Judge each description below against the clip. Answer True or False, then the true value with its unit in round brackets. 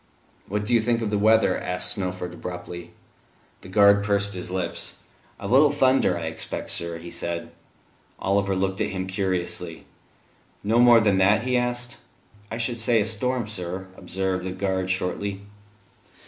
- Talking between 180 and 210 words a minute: False (160 wpm)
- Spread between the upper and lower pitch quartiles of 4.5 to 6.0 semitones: False (3.4 semitones)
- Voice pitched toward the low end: True (100 Hz)